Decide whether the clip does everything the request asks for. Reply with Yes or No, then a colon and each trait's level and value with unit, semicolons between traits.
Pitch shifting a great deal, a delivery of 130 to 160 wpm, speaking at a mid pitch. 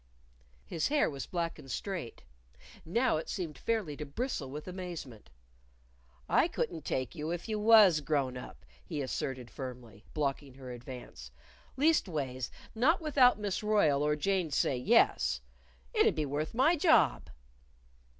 Yes: wide, 7.8 semitones; average, 145 wpm; medium, 155 Hz